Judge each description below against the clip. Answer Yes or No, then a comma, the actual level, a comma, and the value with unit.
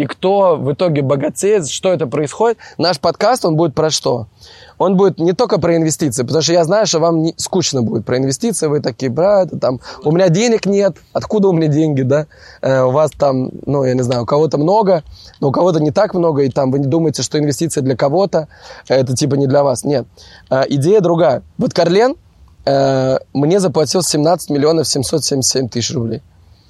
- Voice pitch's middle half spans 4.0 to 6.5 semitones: Yes, average, 5.0 semitones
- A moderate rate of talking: No, fast, 200 wpm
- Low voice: No, medium, 155 Hz